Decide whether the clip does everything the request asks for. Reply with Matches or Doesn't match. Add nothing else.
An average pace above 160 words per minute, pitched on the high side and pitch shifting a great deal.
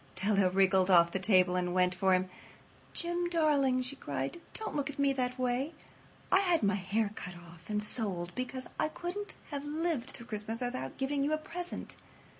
Matches